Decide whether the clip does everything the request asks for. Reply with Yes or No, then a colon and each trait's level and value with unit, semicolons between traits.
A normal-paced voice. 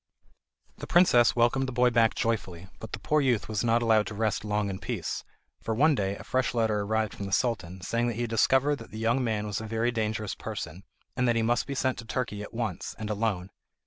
No: fast, 240 wpm